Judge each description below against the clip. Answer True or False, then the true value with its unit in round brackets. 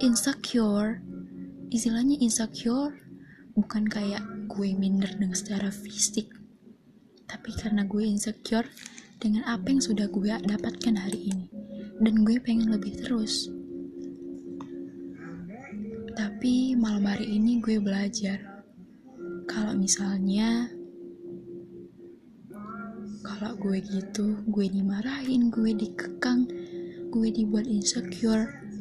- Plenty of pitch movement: False (2.6 semitones)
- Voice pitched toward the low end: False (210 Hz)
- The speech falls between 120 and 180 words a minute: False (95 wpm)